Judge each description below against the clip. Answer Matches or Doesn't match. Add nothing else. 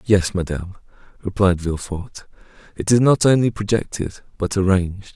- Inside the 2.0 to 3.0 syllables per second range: Doesn't match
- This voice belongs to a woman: Doesn't match